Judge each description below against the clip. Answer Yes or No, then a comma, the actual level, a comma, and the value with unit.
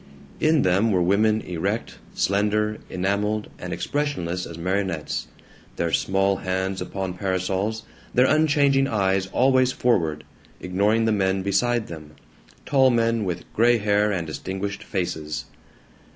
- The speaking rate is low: Yes, slow, 125 wpm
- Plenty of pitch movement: No, average, 3.5 semitones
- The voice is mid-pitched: No, low, 100 Hz